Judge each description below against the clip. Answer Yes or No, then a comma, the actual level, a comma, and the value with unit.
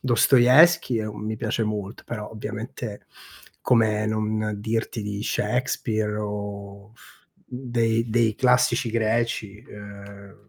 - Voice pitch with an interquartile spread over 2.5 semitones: No, narrow, 2.2 semitones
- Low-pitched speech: Yes, low, 110 Hz